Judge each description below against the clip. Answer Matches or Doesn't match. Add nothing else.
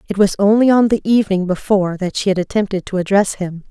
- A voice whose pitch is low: Doesn't match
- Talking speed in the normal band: Doesn't match